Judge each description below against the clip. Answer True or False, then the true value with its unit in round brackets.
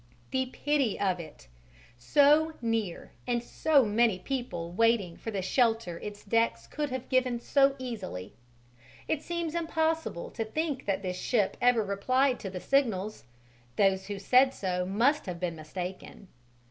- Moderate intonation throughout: False (5.9 semitones)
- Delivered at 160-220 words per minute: False (150 wpm)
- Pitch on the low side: False (230 Hz)